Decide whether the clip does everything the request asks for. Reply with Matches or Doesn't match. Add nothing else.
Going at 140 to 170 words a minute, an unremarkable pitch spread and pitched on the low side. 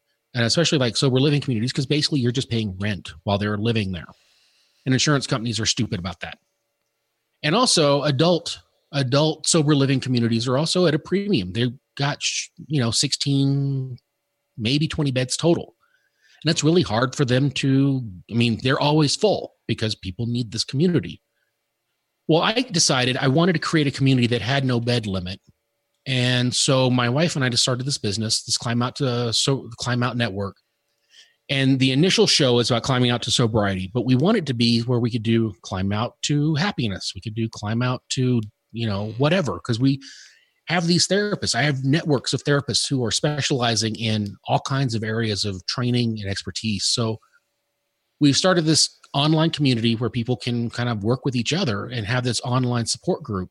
Doesn't match